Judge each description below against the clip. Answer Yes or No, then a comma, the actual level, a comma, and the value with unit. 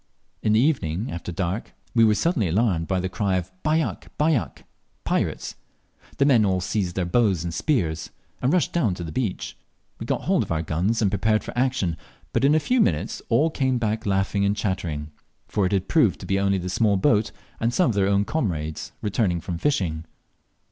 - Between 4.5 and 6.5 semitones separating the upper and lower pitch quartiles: Yes, average, 5.1 semitones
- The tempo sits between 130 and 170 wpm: No, fast, 205 wpm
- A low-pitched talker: Yes, low, 100 Hz